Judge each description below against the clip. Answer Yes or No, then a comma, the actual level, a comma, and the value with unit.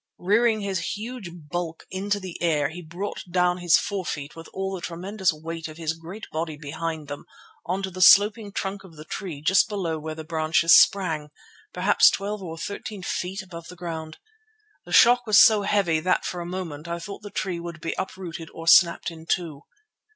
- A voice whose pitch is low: No, medium, 175 Hz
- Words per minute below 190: No, average, 195 wpm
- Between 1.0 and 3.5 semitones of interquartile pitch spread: Yes, average, 3.1 semitones